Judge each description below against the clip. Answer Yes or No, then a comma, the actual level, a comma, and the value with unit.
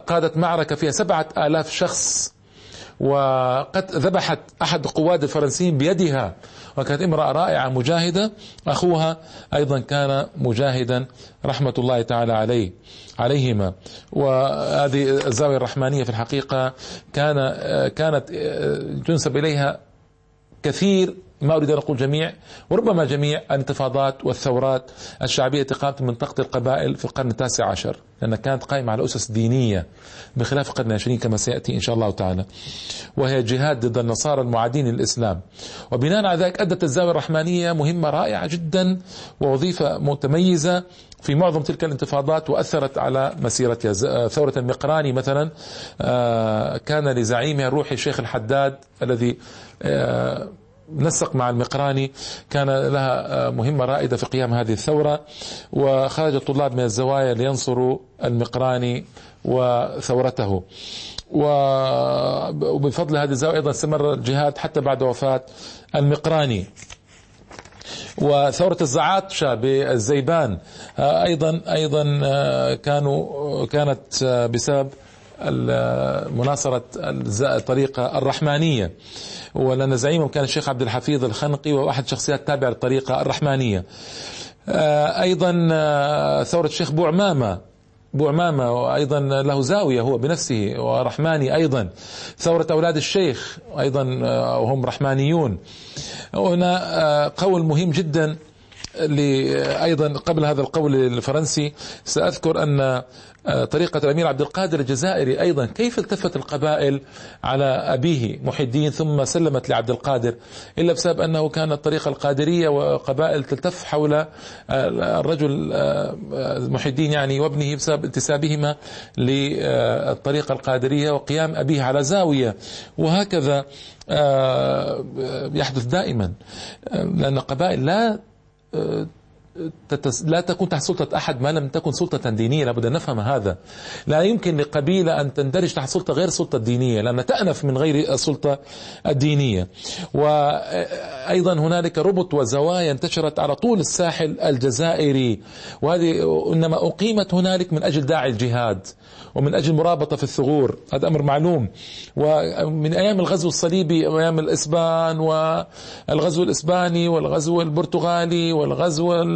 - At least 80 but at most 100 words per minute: No, average, 110 wpm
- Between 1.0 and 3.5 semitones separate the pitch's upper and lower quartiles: No, average, 3.9 semitones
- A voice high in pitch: No, medium, 145 Hz